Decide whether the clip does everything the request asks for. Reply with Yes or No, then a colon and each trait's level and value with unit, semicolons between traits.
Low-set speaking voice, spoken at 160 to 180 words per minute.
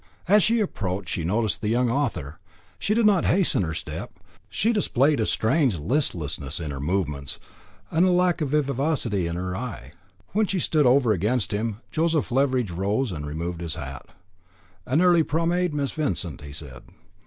Yes: low, 120 Hz; average, 170 wpm